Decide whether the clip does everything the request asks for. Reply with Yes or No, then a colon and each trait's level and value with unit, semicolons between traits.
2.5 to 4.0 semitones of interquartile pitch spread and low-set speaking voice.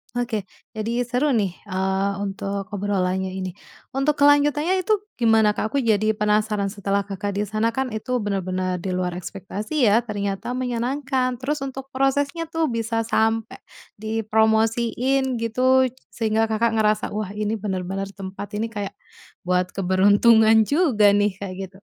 No: average, 3.7 semitones; high, 220 Hz